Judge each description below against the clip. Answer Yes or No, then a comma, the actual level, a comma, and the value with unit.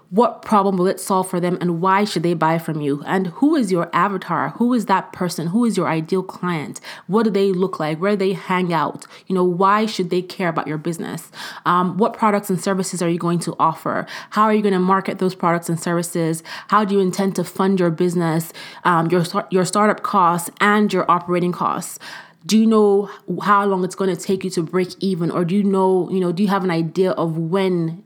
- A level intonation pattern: Yes, narrow, 2.3 semitones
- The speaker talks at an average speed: No, fast, 235 wpm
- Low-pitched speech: No, medium, 185 Hz